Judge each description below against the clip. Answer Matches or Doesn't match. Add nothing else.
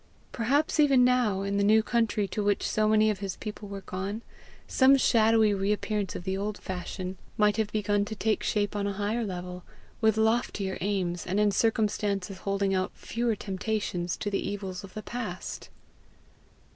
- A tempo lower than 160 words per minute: Doesn't match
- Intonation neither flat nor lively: Doesn't match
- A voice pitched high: Matches